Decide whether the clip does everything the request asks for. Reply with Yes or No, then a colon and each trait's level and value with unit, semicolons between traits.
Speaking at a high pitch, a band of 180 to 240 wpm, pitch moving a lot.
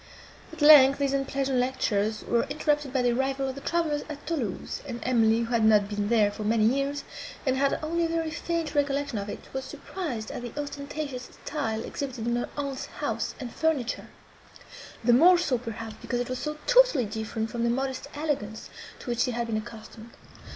No: very high, 260 Hz; average, 195 wpm; average, 4.0 semitones